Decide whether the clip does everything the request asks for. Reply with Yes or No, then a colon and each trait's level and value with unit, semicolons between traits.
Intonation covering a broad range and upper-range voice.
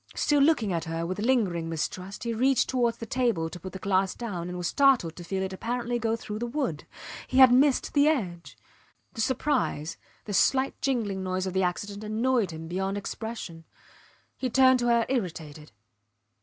Yes: wide, 5.8 semitones; high, 210 Hz